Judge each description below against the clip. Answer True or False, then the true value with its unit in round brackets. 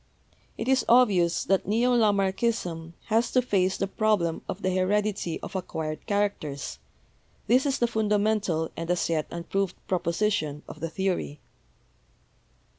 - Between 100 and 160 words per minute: True (140 wpm)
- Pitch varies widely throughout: False (4.2 semitones)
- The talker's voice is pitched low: False (195 Hz)